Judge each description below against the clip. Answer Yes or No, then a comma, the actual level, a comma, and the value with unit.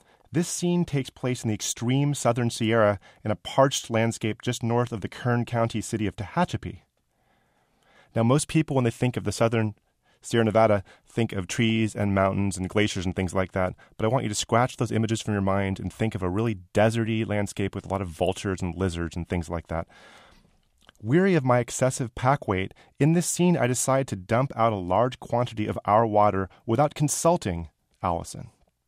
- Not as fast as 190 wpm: No, average, 200 wpm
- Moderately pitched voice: No, low, 110 Hz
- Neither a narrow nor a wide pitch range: Yes, average, 4.0 semitones